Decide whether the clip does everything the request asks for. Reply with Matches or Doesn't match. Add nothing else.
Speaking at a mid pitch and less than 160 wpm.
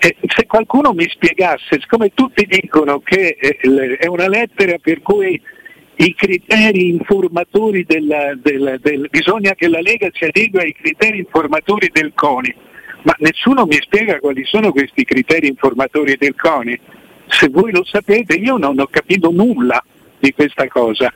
Matches